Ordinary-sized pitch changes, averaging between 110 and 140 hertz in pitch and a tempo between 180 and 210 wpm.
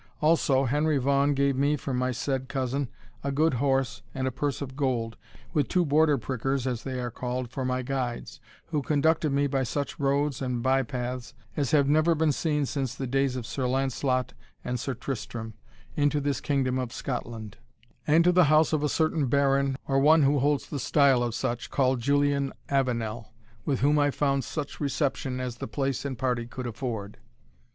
No: narrow, 2.2 semitones; low, 135 Hz; average, 190 wpm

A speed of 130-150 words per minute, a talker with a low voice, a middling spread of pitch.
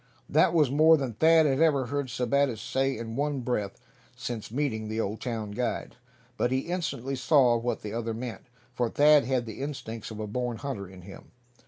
No: average, 195 wpm; low, 125 Hz; average, 3.8 semitones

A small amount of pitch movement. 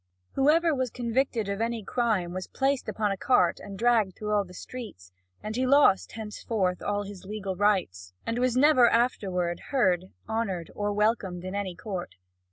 No: average, 4.3 semitones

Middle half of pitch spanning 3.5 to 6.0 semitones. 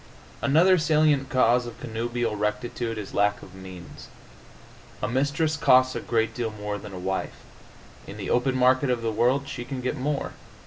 Yes: average, 4.1 semitones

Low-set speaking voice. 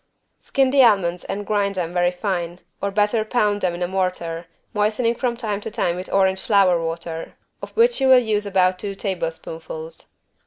No: high, 195 Hz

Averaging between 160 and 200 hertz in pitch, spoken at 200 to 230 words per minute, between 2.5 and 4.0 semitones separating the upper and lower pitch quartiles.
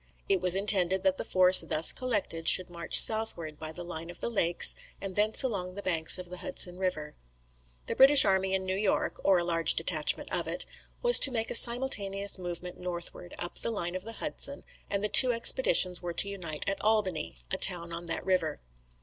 Yes: medium, 185 Hz; fast, 205 wpm; average, 3.1 semitones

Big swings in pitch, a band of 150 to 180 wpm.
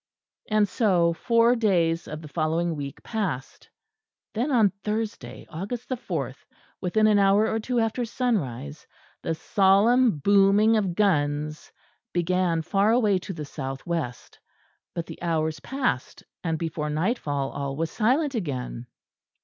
No: wide, 5.9 semitones; average, 140 wpm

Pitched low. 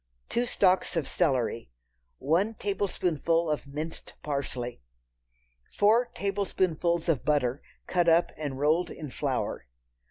No: medium, 165 Hz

